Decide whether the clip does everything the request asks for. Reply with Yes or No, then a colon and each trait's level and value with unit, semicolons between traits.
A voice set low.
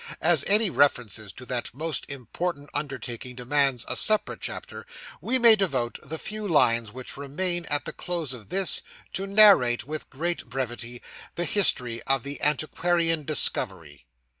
No: medium, 145 Hz